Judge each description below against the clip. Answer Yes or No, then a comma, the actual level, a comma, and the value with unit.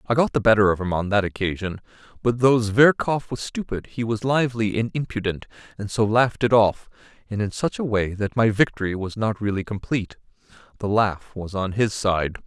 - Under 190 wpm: No, average, 200 wpm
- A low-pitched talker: Yes, low, 110 Hz